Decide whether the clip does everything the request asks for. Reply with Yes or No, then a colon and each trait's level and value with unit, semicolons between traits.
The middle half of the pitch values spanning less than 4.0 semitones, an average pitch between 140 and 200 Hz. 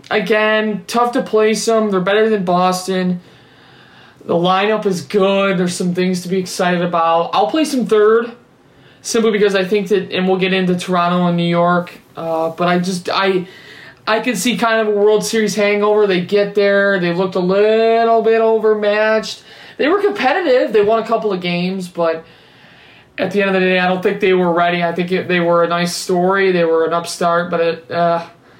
Yes: average, 3.4 semitones; high, 190 Hz